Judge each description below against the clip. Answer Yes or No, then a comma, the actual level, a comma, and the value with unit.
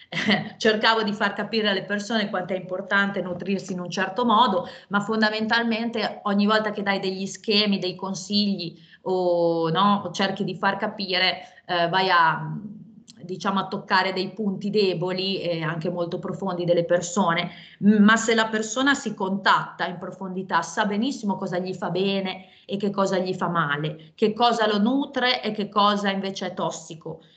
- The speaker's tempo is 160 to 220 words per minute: Yes, average, 165 wpm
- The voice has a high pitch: Yes, high, 195 Hz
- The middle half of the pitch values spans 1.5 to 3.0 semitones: Yes, narrow, 2.6 semitones